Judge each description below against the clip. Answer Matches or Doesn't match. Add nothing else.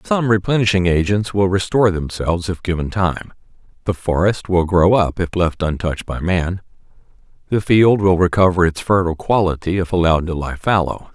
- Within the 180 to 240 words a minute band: Doesn't match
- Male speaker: Matches